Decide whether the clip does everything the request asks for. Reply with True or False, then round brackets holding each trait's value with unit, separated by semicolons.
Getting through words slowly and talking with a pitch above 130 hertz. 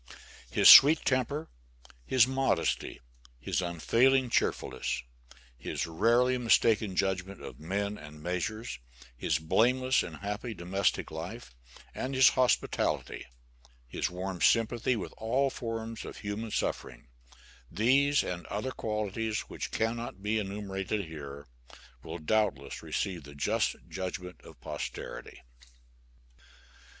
False (115 wpm; 105 Hz)